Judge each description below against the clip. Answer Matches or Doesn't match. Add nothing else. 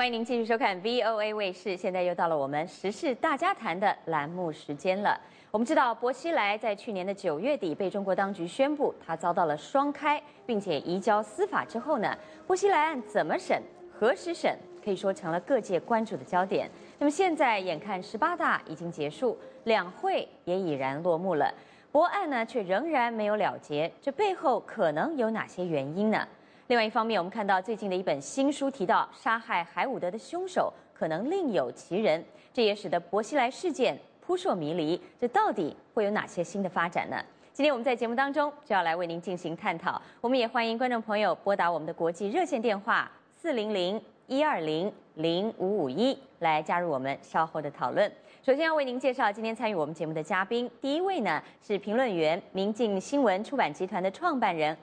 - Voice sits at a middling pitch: Doesn't match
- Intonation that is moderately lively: Doesn't match